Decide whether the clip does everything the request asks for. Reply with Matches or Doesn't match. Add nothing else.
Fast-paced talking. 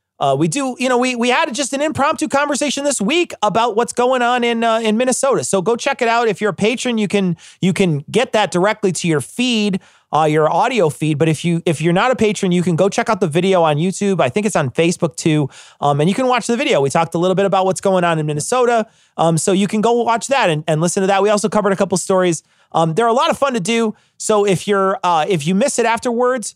Matches